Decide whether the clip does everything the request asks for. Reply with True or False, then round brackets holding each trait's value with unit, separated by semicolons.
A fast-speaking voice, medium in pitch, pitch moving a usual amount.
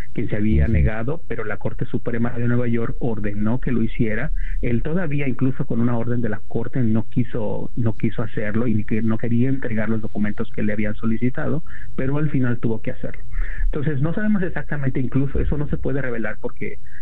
False (195 wpm; 120 Hz; 3.1 semitones)